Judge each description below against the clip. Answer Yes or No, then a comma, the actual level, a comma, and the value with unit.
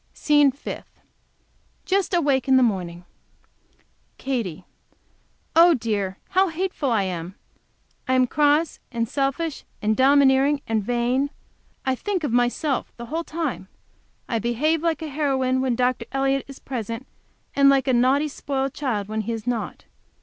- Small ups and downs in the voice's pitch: No, average, 4.0 semitones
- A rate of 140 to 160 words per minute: Yes, average, 150 wpm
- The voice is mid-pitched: No, very high, 265 Hz